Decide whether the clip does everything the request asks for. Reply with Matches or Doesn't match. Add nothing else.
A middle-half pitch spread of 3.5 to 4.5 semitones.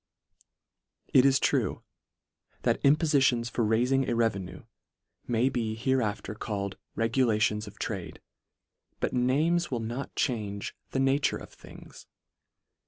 Matches